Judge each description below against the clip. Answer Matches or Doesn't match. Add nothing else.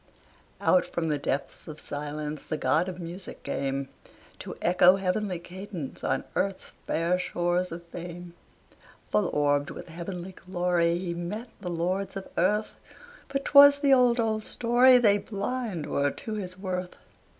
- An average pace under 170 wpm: Matches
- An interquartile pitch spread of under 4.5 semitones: Matches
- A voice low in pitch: Doesn't match